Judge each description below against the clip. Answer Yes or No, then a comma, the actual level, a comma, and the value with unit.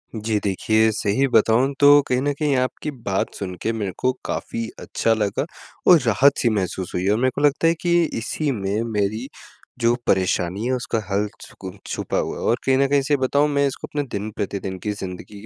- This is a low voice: Yes, low, 115 Hz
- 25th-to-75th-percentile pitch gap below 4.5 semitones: No, average, 5.3 semitones